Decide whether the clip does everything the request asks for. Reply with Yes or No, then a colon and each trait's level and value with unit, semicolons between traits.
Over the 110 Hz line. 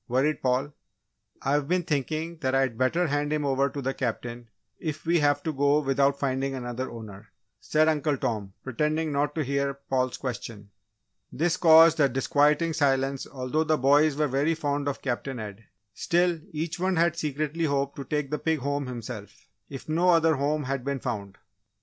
Yes: medium, 140 Hz